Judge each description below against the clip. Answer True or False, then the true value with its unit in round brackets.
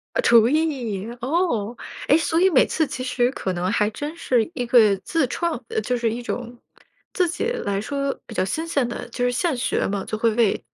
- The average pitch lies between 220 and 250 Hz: True (245 Hz)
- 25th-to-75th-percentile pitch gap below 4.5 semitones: False (5.4 semitones)